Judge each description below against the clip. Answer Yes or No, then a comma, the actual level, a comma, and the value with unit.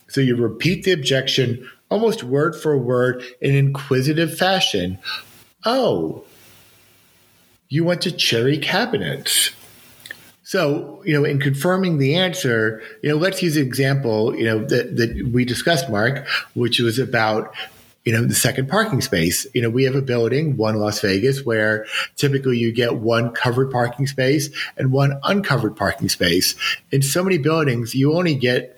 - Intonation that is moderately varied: Yes, average, 4.6 semitones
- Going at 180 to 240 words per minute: No, average, 160 wpm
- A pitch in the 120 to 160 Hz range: Yes, low, 135 Hz